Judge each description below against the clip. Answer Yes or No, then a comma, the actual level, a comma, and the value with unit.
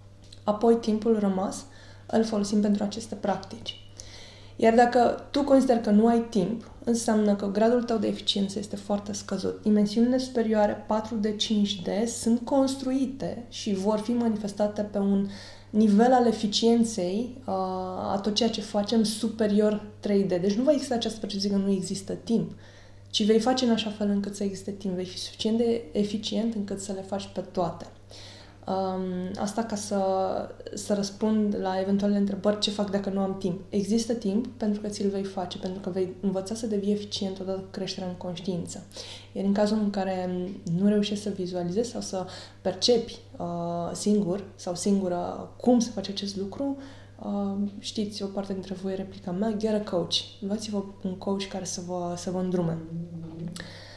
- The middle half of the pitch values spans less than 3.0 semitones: Yes, narrow, 2.6 semitones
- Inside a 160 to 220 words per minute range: Yes, fast, 170 wpm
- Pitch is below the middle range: No, high, 205 Hz